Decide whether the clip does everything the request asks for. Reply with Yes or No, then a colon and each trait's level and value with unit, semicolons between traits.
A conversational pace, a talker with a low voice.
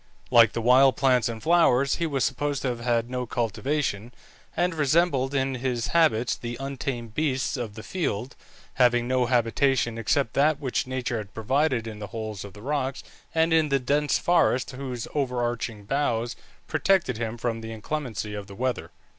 Yes: average, 175 wpm; low, 125 Hz